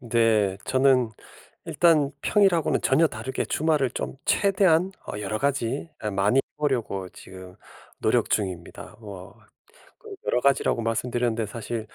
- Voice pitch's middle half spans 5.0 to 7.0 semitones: Yes, wide, 5.5 semitones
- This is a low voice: Yes, low, 120 Hz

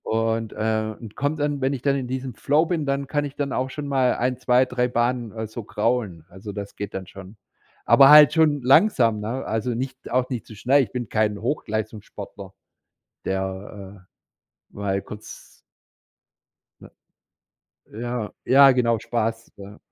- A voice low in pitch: Yes, low, 120 Hz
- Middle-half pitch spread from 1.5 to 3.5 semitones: No, average, 4.0 semitones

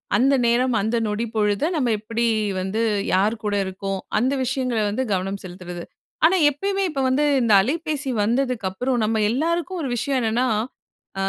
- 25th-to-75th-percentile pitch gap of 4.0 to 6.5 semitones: Yes, average, 4.7 semitones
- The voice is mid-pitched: No, high, 235 Hz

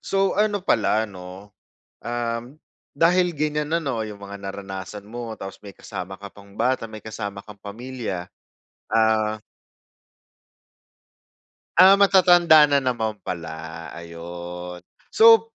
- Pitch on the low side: Yes, low, 110 Hz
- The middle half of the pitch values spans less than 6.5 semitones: No, wide, 7.5 semitones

